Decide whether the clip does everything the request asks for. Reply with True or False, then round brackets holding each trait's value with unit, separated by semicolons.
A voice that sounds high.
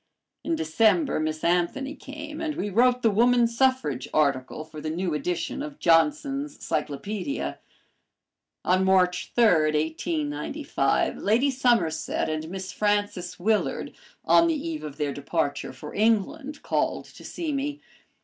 True (205 Hz)